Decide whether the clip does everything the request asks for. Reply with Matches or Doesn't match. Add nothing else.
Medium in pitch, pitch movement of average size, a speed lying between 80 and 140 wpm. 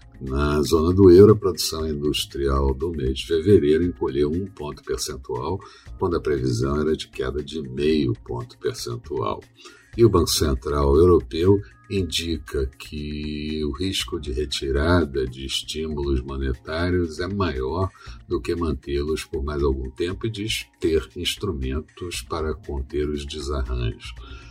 Doesn't match